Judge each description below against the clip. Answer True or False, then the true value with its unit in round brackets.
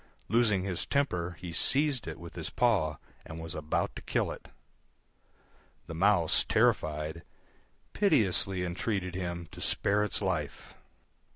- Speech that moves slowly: True (130 wpm)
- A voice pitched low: True (90 Hz)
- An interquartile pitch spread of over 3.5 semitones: True (4.1 semitones)